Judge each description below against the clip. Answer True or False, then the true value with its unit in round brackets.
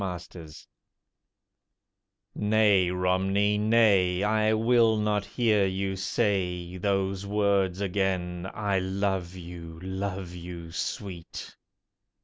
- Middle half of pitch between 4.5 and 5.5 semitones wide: False (2.4 semitones)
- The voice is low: True (95 Hz)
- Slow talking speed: True (90 wpm)